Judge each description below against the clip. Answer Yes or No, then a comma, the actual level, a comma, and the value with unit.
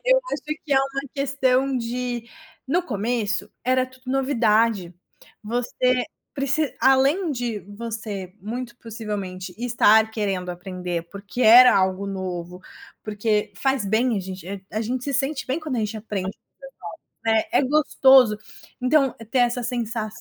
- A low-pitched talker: No, high, 235 Hz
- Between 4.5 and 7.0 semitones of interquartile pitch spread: No, average, 4.0 semitones